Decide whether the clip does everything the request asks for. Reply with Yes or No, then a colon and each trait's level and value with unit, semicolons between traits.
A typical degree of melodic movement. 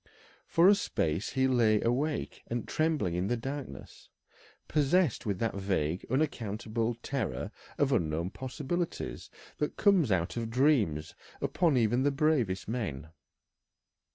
No: wide, 6.8 semitones